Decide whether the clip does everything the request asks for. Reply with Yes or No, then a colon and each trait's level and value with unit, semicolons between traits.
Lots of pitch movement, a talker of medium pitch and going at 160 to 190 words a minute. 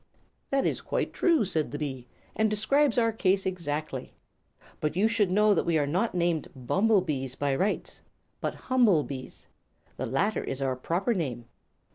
Yes: wide, 6.8 semitones; medium, 180 Hz; average, 170 wpm